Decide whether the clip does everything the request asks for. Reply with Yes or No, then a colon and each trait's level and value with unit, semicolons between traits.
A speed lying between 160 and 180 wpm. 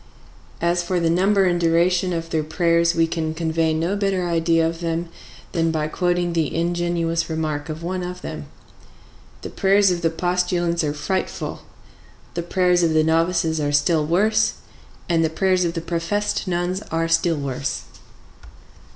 Yes: average, 165 wpm